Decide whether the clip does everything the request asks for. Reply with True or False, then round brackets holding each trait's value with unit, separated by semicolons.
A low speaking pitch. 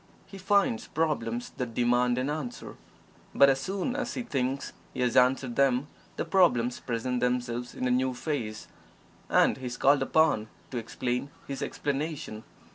True (130 Hz)